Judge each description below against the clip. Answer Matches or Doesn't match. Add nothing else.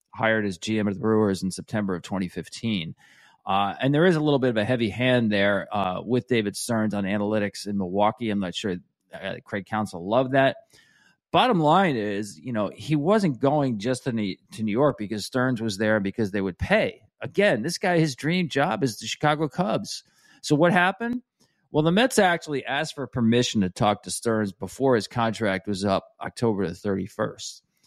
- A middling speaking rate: Matches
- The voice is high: Doesn't match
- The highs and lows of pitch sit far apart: Matches